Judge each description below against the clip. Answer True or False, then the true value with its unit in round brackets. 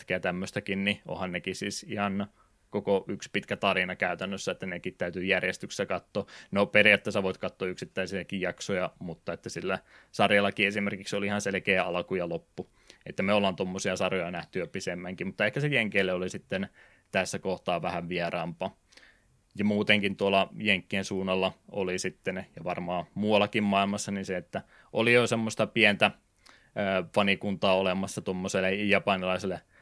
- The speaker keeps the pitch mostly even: True (1.6 semitones)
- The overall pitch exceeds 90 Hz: True (100 Hz)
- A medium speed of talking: True (145 wpm)